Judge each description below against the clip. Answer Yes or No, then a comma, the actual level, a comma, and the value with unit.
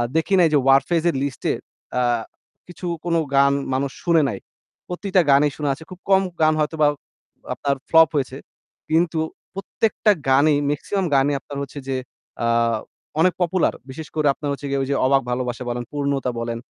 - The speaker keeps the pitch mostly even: No, average, 3.5 semitones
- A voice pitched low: No, medium, 145 Hz